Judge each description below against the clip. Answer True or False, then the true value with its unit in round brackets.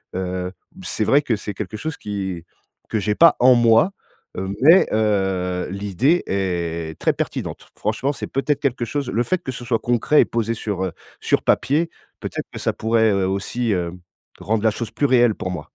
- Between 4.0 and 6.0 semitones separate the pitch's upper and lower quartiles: True (4.6 semitones)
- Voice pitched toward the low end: True (110 Hz)